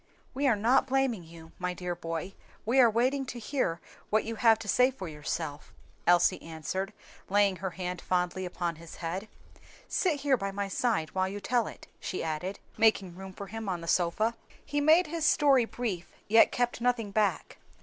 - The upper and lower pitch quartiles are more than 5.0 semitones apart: Yes, wide, 5.4 semitones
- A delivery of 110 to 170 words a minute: No, average, 190 wpm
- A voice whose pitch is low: No, high, 200 Hz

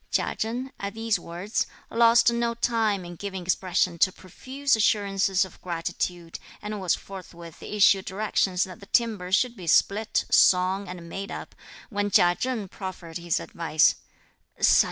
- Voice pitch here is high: Yes, high, 195 Hz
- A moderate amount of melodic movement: Yes, average, 3.4 semitones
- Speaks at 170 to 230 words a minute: No, average, 150 wpm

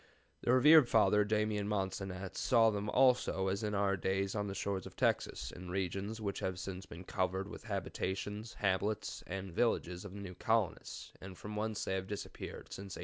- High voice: No, low, 100 Hz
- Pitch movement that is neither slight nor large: No, narrow, 2.0 semitones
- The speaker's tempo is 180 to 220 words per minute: Yes, average, 195 wpm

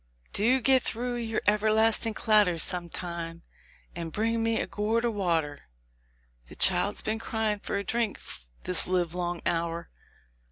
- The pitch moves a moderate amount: Yes, average, 4.6 semitones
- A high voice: Yes, high, 210 Hz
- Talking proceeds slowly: No, average, 145 wpm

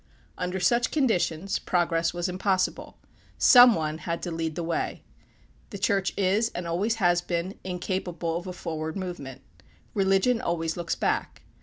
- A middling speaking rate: Yes, average, 150 wpm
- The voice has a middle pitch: Yes, medium, 180 Hz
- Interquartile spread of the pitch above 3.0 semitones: No, narrow, 2.5 semitones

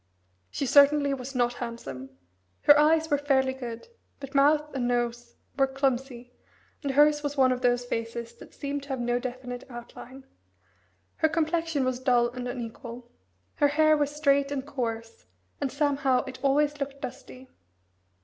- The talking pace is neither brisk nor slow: Yes, average, 160 wpm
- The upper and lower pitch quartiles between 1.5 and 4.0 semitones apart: Yes, average, 2.8 semitones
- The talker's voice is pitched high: Yes, very high, 265 Hz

